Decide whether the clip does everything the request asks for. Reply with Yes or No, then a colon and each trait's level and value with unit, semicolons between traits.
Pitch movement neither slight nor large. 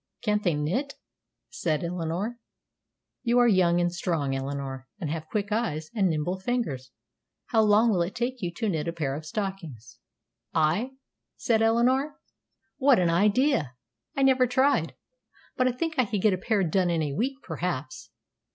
No: wide, 7.1 semitones